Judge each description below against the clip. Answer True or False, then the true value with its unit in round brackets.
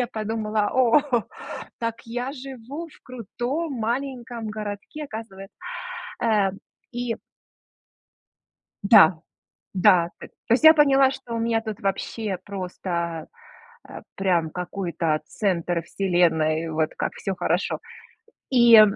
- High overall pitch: True (220 Hz)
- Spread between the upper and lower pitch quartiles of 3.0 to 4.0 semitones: False (5.0 semitones)